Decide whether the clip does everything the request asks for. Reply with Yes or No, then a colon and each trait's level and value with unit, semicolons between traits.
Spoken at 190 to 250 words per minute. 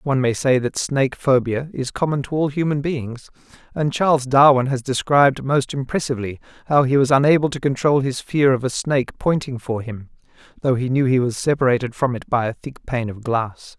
Yes: average, 200 wpm